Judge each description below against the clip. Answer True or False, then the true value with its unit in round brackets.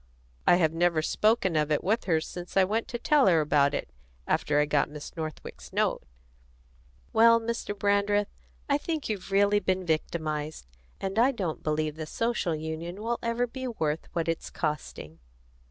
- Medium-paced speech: True (170 wpm)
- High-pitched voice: False (180 Hz)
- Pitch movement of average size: False (6.1 semitones)